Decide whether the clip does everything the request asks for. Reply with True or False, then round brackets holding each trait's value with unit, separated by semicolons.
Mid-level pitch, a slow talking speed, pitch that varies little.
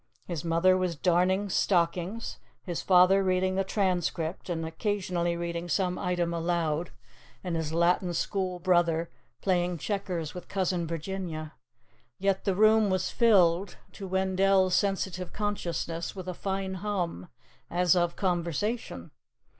True (180 Hz; 130 wpm; 2.1 semitones)